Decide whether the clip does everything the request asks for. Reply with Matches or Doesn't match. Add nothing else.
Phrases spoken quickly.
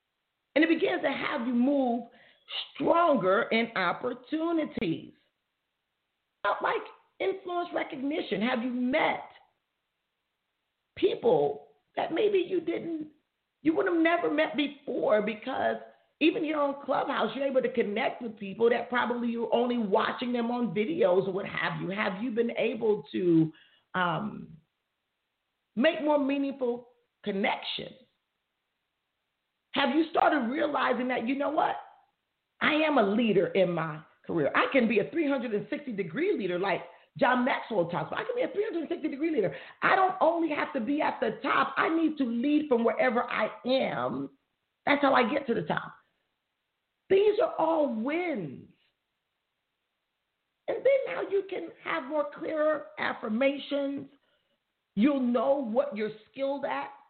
Doesn't match